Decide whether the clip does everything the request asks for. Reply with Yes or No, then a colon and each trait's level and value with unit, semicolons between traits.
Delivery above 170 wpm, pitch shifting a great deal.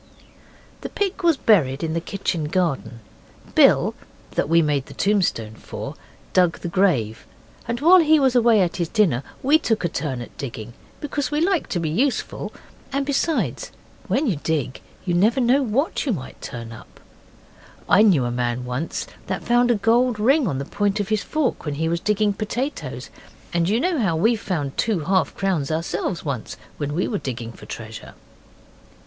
Yes: average, 185 wpm; wide, 8.7 semitones